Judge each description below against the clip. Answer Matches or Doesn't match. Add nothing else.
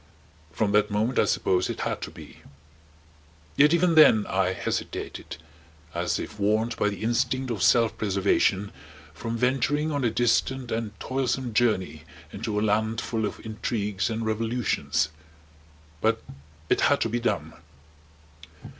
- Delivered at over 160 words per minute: Doesn't match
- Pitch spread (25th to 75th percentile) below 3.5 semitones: Matches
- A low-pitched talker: Matches